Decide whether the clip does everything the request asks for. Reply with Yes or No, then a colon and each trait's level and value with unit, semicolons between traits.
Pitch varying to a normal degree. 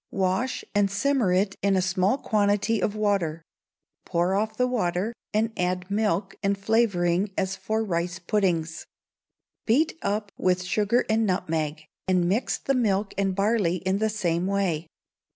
Yes: average, 3.0 semitones